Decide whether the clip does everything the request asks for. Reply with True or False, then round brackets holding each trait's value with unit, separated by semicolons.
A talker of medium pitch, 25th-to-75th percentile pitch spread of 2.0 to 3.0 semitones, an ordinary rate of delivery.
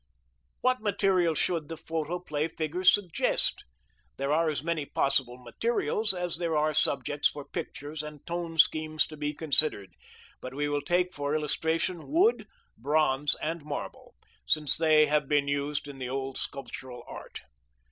True (155 Hz; 2.7 semitones; 150 wpm)